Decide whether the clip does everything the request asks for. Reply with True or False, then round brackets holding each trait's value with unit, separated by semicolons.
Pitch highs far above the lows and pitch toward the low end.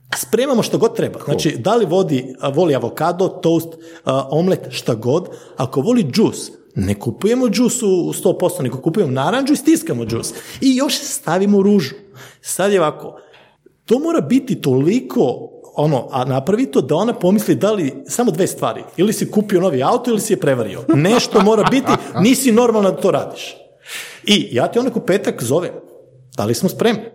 False (6.7 semitones; 190 Hz)